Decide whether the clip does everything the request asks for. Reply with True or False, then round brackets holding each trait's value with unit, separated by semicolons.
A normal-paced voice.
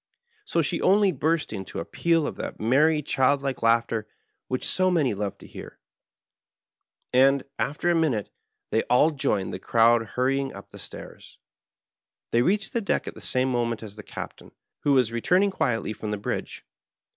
True (175 wpm)